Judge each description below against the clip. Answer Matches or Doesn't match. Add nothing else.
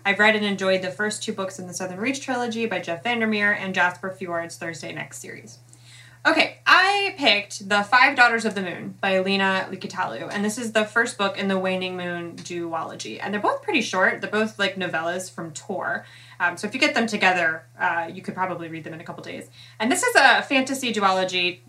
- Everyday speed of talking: Doesn't match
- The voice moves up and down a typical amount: Matches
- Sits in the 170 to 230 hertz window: Matches